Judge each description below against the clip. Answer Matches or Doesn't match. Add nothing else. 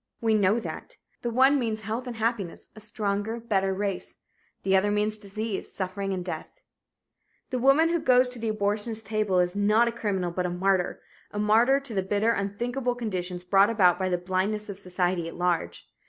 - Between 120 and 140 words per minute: Doesn't match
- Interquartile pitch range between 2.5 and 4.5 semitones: Matches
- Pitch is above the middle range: Matches